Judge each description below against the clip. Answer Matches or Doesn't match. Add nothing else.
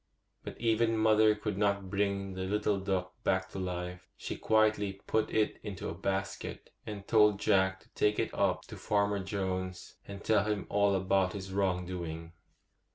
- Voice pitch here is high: Doesn't match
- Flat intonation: Matches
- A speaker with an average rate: Matches